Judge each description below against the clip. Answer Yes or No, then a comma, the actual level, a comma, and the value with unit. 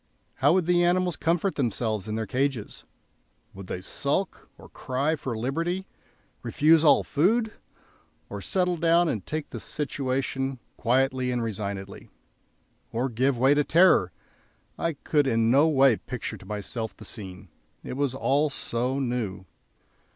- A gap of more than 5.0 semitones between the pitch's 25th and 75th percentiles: Yes, wide, 5.5 semitones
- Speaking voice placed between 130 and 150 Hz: Yes, low, 135 Hz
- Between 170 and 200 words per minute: No, average, 145 wpm